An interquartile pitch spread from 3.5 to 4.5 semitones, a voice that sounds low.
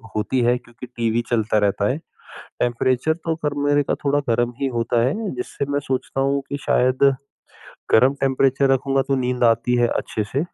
No: average, 2.7 semitones; low, 130 Hz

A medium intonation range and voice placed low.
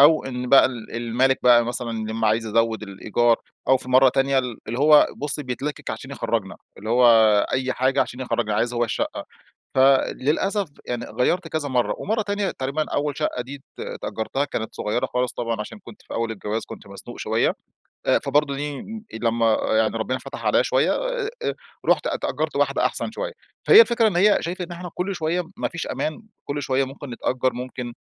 Yes: average, 4.2 semitones; low, 130 Hz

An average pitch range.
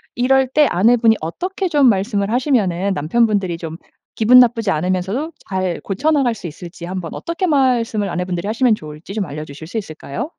No: wide, 5.9 semitones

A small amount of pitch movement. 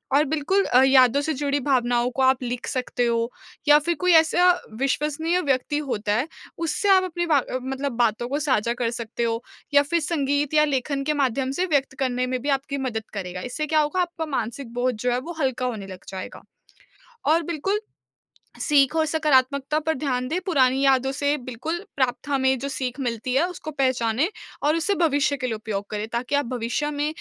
No: average, 3.5 semitones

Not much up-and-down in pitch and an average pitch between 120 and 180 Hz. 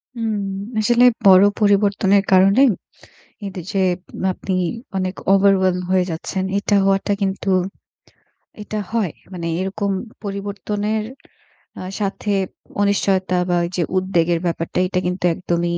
No: narrow, 1.7 semitones; high, 195 Hz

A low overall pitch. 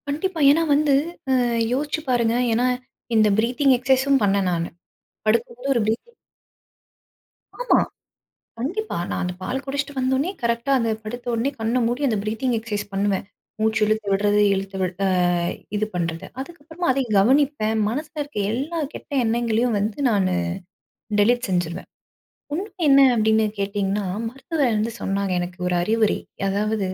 No: high, 230 Hz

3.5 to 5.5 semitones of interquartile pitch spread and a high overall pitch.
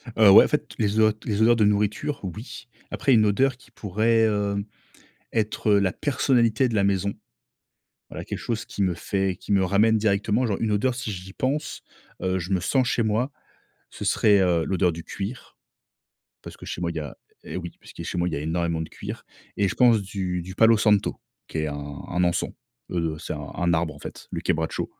No: average, 3.8 semitones; low, 100 Hz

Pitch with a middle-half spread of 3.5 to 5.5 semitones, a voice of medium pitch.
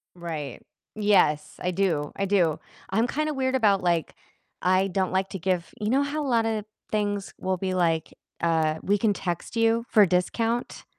No: average, 4.4 semitones; high, 195 Hz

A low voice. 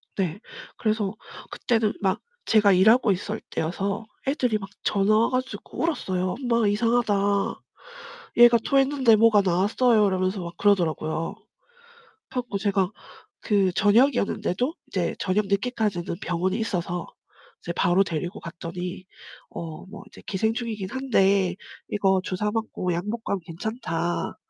No: high, 200 Hz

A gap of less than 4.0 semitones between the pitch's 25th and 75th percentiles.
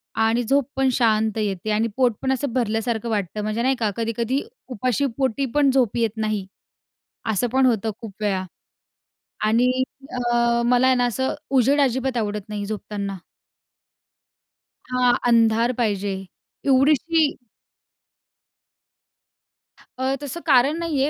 Yes: average, 3.4 semitones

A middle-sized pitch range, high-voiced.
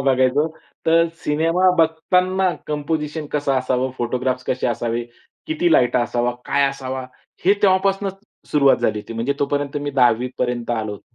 No: average, 4.4 semitones; medium, 140 Hz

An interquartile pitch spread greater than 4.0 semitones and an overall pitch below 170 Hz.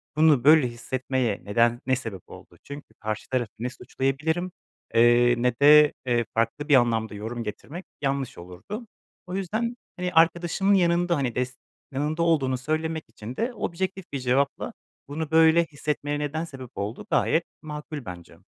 Yes: average, 5.1 semitones; medium, 140 Hz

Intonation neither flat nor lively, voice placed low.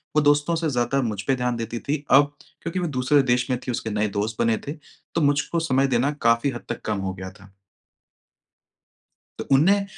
Yes: average, 4.0 semitones; low, 130 Hz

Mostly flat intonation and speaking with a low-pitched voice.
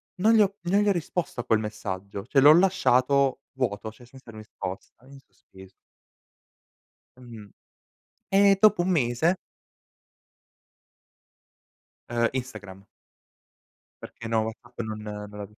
No: wide, 7.8 semitones; low, 120 Hz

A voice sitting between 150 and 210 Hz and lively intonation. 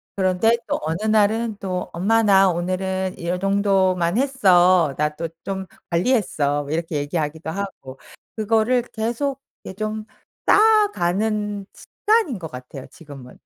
No: high, 190 Hz; average, 4.6 semitones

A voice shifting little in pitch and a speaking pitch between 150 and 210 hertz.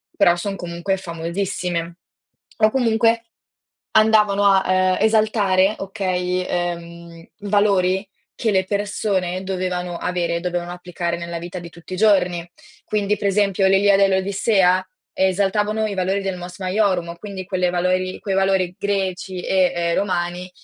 Yes: narrow, 2.2 semitones; medium, 185 Hz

